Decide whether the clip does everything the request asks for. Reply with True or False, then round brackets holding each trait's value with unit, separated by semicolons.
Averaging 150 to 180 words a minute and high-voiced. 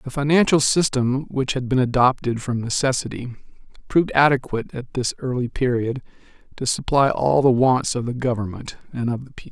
False (170 wpm; 130 Hz)